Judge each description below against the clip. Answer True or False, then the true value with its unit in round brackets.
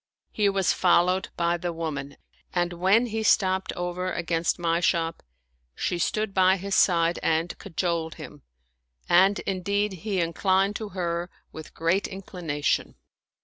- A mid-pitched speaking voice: True (180 Hz)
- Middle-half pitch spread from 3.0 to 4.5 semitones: False (2.4 semitones)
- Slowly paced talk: False (145 wpm)